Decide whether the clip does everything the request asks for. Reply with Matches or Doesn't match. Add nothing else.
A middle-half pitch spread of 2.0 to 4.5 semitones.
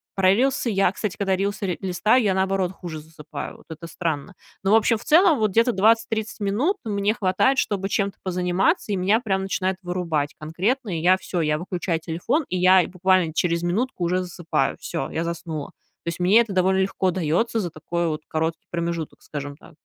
Matches